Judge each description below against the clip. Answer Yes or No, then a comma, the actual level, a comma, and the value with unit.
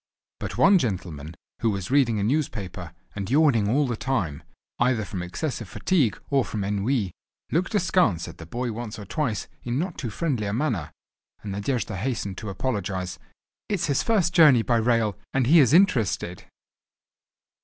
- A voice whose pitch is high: No, low, 115 Hz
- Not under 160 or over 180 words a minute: Yes, average, 165 wpm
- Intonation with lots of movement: Yes, wide, 6.0 semitones